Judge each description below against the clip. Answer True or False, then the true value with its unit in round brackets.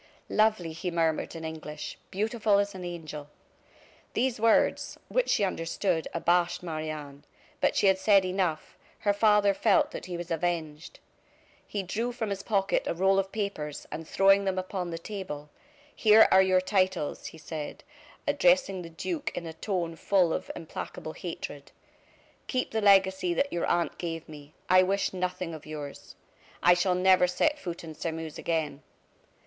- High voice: False (180 Hz)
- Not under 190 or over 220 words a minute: False (165 wpm)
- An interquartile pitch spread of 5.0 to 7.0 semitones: False (3.6 semitones)